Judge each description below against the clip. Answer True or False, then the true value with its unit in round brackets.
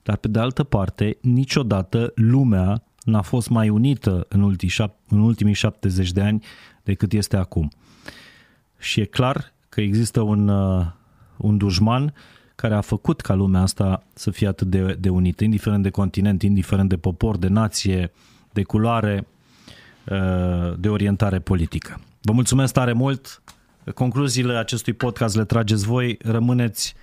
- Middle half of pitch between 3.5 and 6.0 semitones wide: False (3.1 semitones)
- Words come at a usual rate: True (140 wpm)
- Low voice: True (105 Hz)